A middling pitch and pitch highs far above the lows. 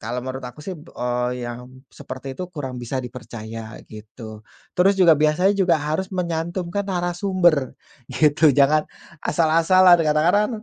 Yes: medium, 155 Hz; wide, 6.1 semitones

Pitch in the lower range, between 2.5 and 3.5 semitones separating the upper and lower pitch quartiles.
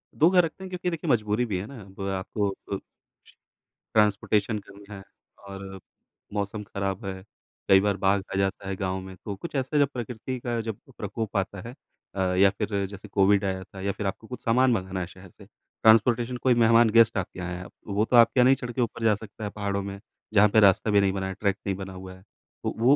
Yes: low, 100 Hz; average, 3.1 semitones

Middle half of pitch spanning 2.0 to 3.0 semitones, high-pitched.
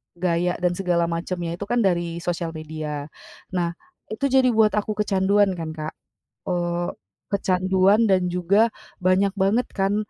No: average, 2.7 semitones; medium, 180 Hz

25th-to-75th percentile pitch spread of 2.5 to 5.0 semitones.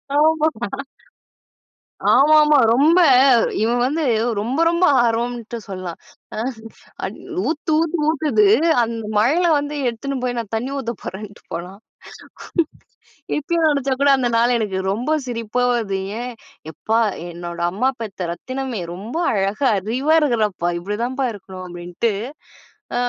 No: wide, 5.6 semitones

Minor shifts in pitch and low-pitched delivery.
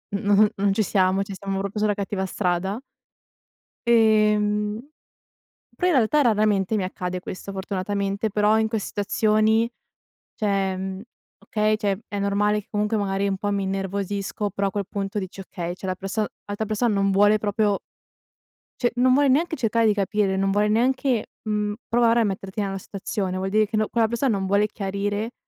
No: narrow, 1.8 semitones; high, 205 Hz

